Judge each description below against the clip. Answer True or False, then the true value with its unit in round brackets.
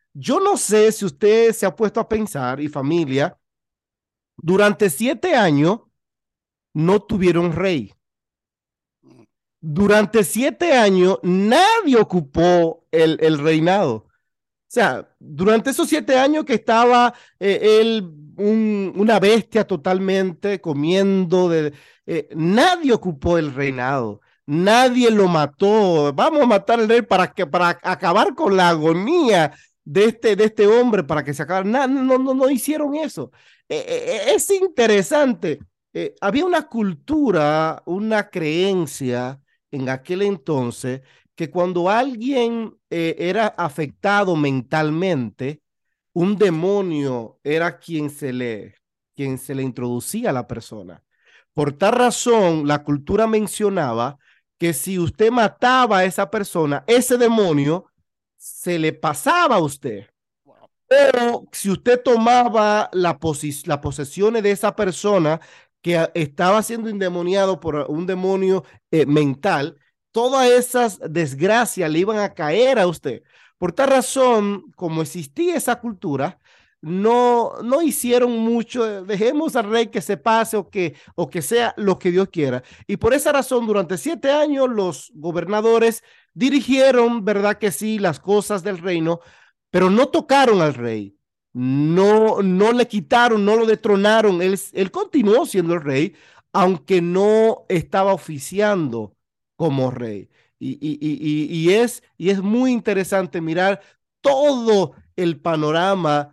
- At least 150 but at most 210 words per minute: False (135 wpm)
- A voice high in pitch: True (195 Hz)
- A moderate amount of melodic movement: False (6.1 semitones)